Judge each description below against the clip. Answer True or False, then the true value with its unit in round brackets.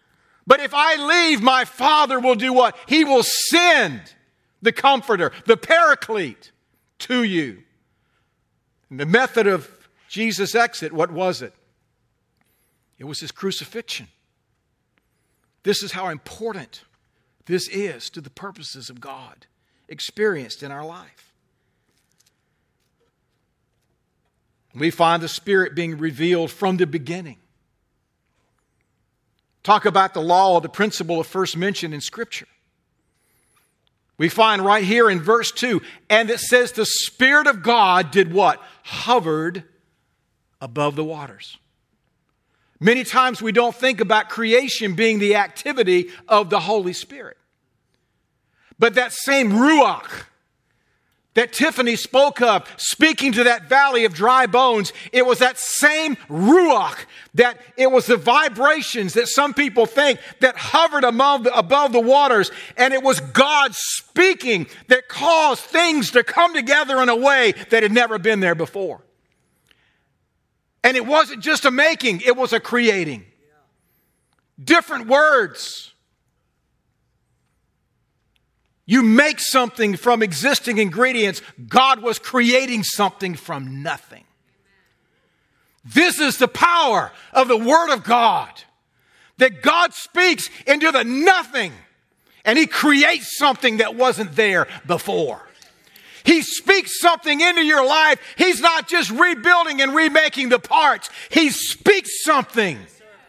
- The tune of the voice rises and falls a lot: True (6.5 semitones)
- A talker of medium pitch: False (240 Hz)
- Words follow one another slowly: True (125 wpm)